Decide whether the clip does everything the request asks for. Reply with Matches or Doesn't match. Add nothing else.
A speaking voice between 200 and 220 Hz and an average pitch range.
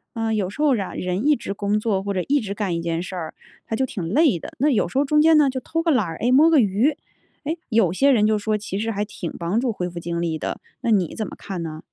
Doesn't match